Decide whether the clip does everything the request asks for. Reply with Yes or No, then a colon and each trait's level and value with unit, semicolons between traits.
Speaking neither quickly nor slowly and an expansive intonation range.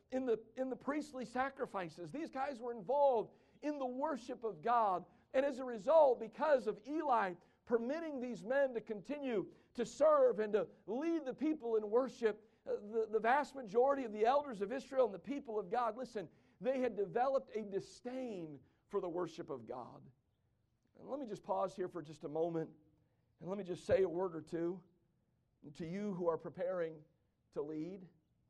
Yes: average, 185 wpm; wide, 6.4 semitones